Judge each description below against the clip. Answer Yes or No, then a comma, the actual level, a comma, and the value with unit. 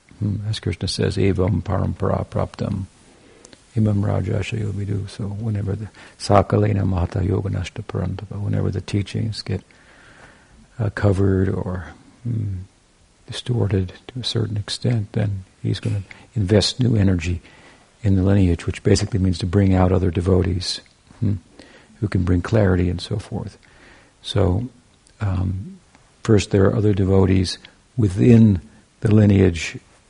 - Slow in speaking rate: Yes, slow, 130 wpm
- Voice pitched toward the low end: Yes, low, 100 Hz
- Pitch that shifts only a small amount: Yes, narrow, 2.3 semitones